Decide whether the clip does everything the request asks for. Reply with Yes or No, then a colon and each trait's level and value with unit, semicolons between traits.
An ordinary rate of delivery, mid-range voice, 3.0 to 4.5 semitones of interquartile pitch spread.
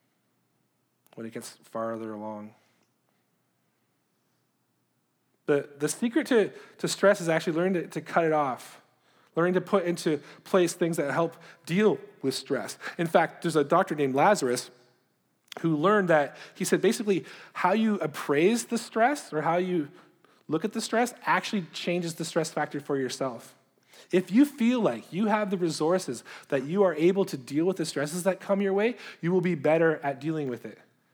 No: average, 175 wpm; medium, 170 Hz; average, 5.1 semitones